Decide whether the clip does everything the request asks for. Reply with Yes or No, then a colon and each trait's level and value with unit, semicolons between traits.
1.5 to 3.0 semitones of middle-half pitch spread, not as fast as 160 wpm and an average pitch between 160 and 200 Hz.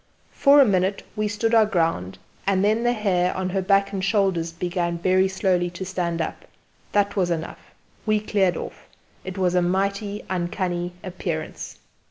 No: narrow, 2.4 semitones; average, 170 wpm; high, 190 Hz